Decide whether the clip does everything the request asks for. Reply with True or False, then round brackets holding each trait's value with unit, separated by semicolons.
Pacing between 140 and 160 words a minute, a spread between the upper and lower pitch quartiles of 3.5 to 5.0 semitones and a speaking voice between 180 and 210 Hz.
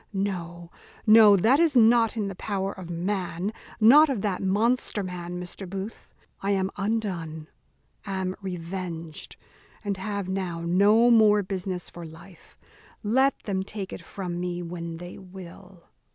False (145 wpm; 2.9 semitones; 190 Hz)